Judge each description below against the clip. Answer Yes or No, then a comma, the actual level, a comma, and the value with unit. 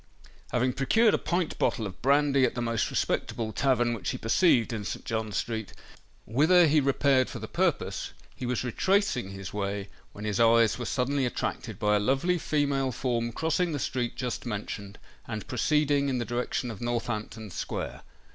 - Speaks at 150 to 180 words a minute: Yes, average, 175 wpm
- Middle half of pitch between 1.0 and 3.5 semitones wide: No, average, 4.1 semitones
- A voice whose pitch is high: No, low, 120 Hz